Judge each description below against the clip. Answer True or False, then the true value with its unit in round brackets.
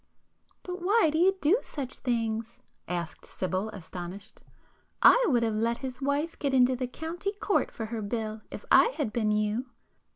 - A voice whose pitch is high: True (245 Hz)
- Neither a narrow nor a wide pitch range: False (6.6 semitones)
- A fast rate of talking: False (170 wpm)